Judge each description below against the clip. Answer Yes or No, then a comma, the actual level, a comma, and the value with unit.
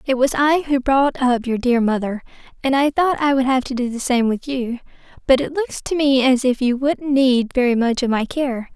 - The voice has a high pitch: Yes, very high, 260 Hz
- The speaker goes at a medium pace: No, fast, 245 wpm